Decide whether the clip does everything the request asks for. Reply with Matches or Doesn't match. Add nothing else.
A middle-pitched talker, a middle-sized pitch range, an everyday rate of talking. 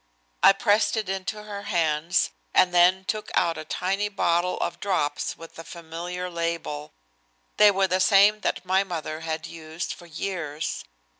Matches